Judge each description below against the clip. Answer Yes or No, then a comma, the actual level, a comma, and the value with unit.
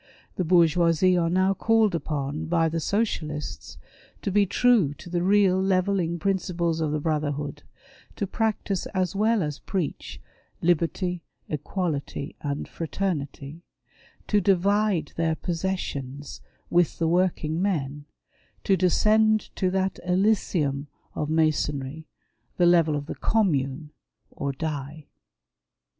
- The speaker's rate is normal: No, slow, 125 wpm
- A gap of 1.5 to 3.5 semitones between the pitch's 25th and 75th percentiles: No, average, 4.1 semitones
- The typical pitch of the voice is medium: Yes, medium, 170 Hz